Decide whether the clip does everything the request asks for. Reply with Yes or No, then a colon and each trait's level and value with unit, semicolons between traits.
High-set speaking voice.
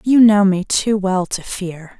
Yes: high, 195 Hz